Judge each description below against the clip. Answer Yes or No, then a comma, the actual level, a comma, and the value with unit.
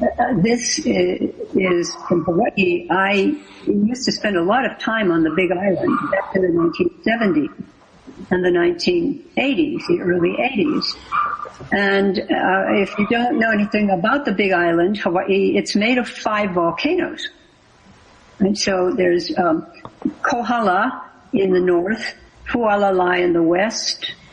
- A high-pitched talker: Yes, high, 200 Hz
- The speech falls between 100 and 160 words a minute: Yes, average, 140 wpm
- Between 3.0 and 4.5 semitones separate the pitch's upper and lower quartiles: No, average, 5.3 semitones